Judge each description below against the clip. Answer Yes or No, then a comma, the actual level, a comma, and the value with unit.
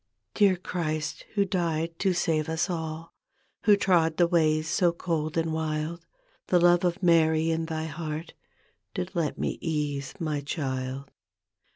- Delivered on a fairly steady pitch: Yes, narrow, 1.9 semitones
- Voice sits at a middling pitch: Yes, medium, 160 Hz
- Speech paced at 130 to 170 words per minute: Yes, average, 150 wpm